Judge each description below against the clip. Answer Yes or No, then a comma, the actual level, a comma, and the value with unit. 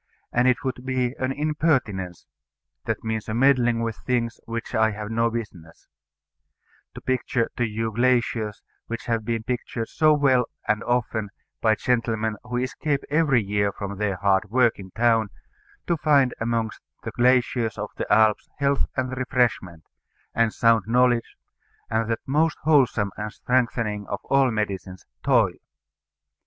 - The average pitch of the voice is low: Yes, low, 115 Hz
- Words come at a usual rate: Yes, average, 150 wpm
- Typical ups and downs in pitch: Yes, average, 3.0 semitones